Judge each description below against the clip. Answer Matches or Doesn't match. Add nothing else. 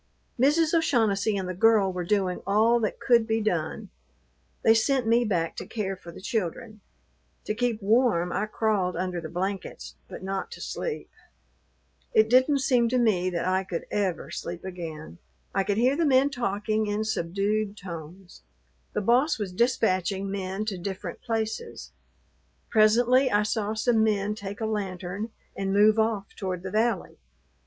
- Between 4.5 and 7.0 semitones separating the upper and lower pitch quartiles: Doesn't match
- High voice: Matches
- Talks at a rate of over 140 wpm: Matches